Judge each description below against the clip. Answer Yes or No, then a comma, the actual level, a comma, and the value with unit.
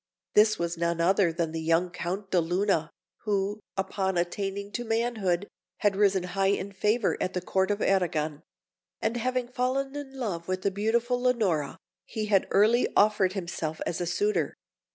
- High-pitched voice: Yes, high, 195 Hz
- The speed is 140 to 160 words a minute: No, average, 170 wpm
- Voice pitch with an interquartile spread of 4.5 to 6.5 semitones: No, average, 3.9 semitones